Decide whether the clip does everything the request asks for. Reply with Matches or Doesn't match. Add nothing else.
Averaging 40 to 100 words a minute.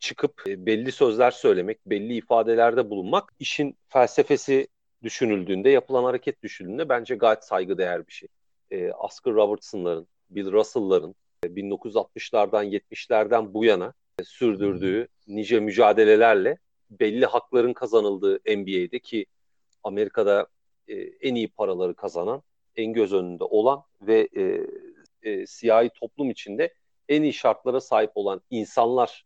Doesn't match